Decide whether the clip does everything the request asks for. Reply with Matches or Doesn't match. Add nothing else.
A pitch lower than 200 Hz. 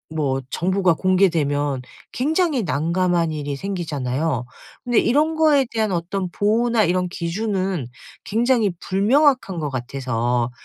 Matches